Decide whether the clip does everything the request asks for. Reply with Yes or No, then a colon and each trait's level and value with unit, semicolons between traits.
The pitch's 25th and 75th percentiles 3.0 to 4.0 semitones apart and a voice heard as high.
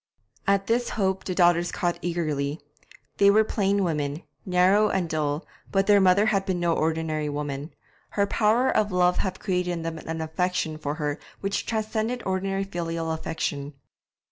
No: average, 3.7 semitones; medium, 180 Hz